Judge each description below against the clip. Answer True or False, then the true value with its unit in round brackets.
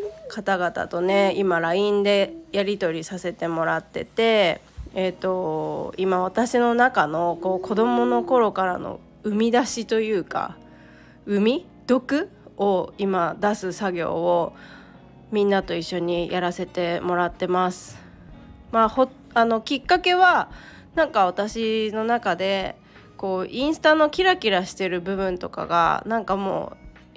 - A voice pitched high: True (195 Hz)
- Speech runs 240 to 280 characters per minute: True (255 characters per minute)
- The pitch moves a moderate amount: True (4.2 semitones)